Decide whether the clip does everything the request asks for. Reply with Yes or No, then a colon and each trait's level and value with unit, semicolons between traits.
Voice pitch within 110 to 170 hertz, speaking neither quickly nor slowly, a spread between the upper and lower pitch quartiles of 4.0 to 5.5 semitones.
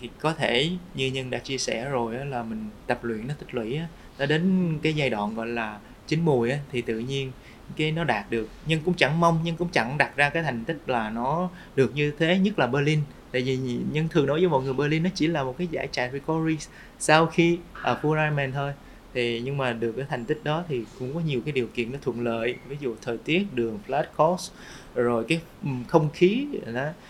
Yes: medium, 140 Hz; average, 235 wpm; average, 4.8 semitones